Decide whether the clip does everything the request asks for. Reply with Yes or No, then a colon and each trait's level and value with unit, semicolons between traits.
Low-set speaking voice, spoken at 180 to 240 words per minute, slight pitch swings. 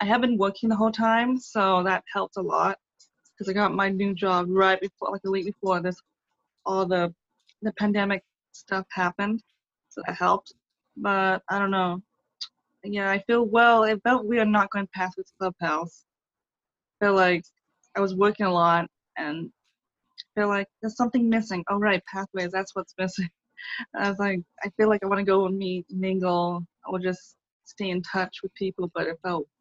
No: high, 195 Hz; average, 200 wpm; narrow, 2.3 semitones